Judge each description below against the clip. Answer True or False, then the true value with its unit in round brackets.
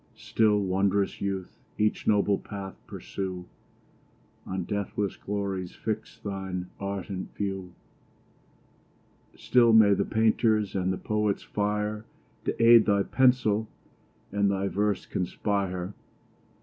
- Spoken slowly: True (110 wpm)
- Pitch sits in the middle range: False (100 Hz)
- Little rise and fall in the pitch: True (1.7 semitones)